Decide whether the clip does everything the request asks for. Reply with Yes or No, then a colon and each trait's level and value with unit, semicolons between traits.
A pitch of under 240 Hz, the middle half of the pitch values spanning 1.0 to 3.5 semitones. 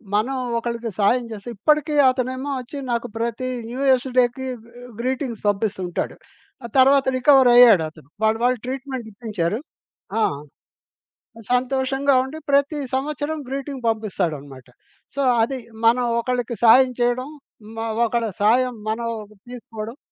No: high, 245 Hz; average, 2.9 semitones